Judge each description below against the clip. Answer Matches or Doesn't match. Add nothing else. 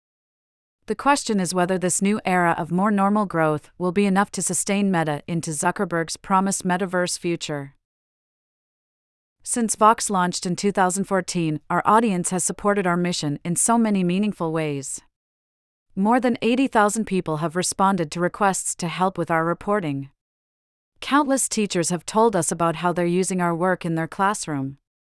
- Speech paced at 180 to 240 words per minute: Doesn't match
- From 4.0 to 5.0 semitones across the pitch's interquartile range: Doesn't match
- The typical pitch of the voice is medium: Matches